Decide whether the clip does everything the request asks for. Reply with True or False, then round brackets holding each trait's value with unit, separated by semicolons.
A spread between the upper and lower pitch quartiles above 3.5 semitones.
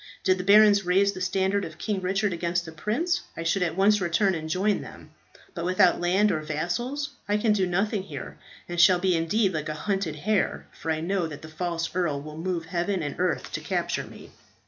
False (3.2 semitones)